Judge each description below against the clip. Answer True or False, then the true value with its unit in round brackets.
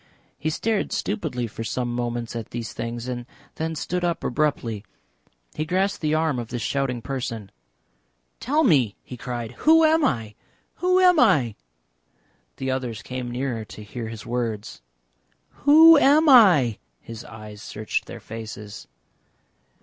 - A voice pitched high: False (125 Hz)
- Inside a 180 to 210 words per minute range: False (145 wpm)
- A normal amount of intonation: False (7.0 semitones)